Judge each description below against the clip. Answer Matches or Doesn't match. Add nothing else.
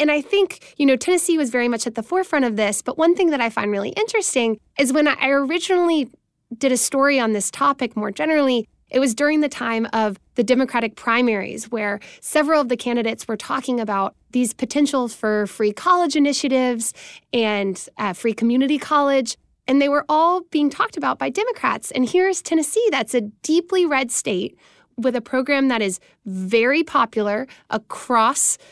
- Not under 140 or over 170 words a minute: Doesn't match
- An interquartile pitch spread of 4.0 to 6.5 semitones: Matches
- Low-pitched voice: Doesn't match